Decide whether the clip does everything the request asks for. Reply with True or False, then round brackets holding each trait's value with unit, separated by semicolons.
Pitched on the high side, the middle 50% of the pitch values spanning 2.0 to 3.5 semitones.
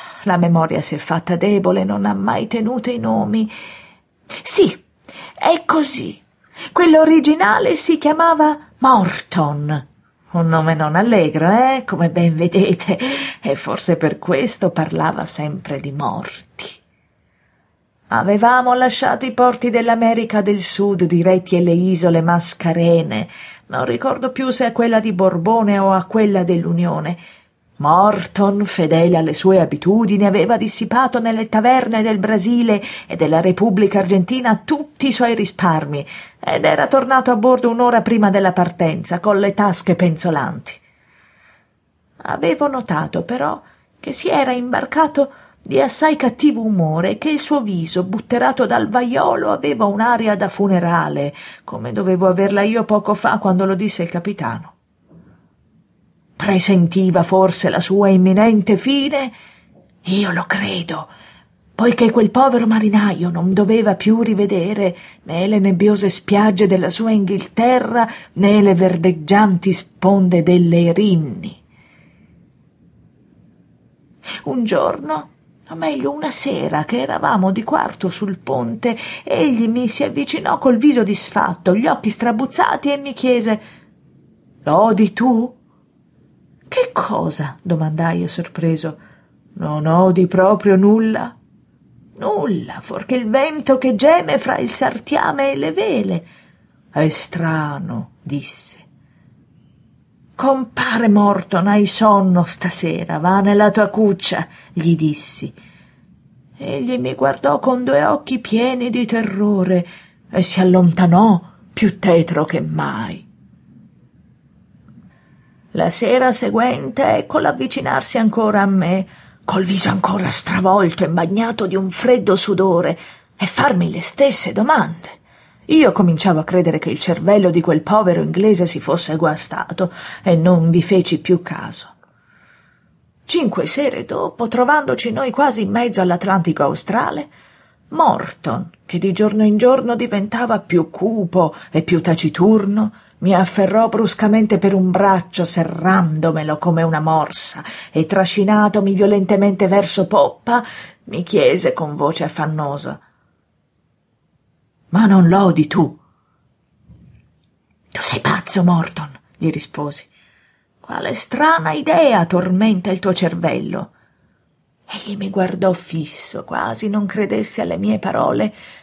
False (195 Hz; 4.7 semitones)